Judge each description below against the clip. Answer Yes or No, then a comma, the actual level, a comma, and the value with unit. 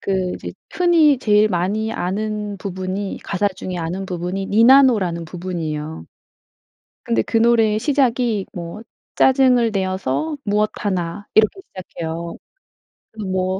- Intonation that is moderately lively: Yes, average, 3.8 semitones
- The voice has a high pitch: Yes, high, 200 Hz